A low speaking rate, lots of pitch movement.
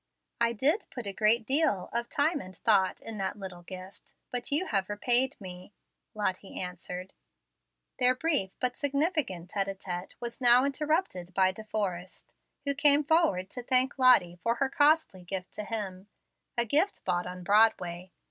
No: average, 165 wpm; wide, 6.1 semitones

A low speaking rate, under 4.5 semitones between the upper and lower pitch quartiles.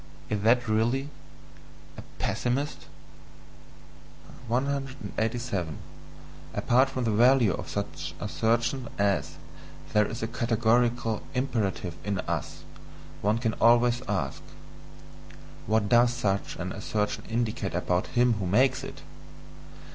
Yes: slow, 110 wpm; average, 2.8 semitones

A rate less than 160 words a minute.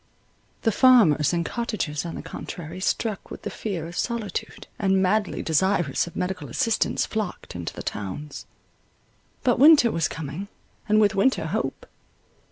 Yes: average, 150 wpm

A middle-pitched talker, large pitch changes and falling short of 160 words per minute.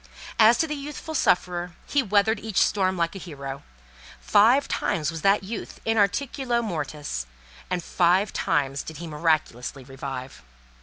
Yes: medium, 180 Hz; wide, 6.8 semitones; average, 150 wpm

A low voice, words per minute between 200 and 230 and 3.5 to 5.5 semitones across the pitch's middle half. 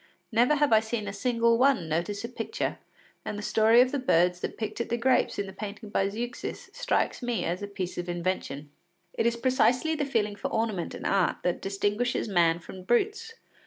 No: high, 220 Hz; fast, 205 wpm; average, 4.2 semitones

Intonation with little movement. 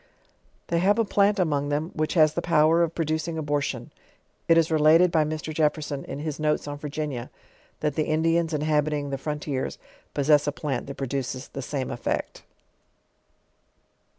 Yes: narrow, 1.9 semitones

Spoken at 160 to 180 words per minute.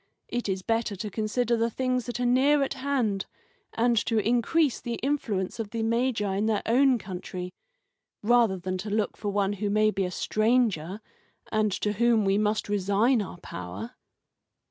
Yes: average, 175 wpm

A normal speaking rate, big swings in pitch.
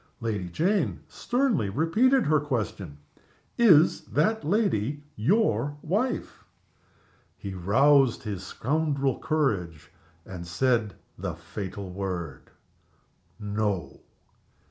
No: slow, 90 wpm; wide, 8.6 semitones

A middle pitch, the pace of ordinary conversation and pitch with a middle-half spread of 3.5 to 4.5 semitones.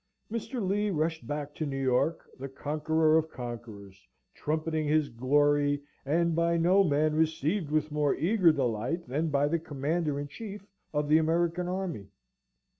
No: medium, 155 Hz; average, 155 wpm; average, 2.8 semitones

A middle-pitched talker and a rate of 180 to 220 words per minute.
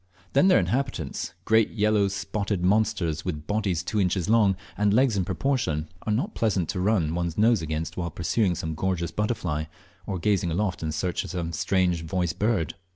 No: very low, 95 Hz; average, 185 wpm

